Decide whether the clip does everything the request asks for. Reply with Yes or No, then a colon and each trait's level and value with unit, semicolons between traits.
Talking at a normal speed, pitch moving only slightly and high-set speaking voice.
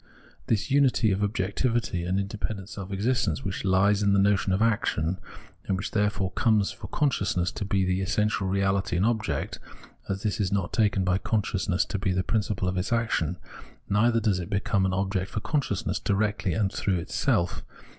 No: average, 185 wpm; narrow, 2.3 semitones; low, 100 Hz